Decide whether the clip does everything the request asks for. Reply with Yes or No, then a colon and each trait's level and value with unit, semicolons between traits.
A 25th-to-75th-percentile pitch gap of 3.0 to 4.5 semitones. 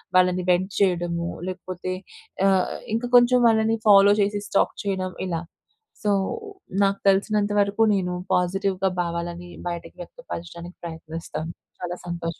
No: narrow, 2.6 semitones